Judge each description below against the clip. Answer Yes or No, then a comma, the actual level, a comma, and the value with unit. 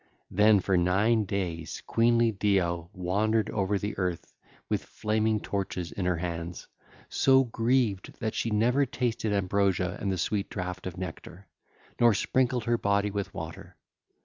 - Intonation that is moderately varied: Yes, average, 3.4 semitones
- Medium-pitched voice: No, low, 100 Hz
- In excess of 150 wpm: No, average, 145 wpm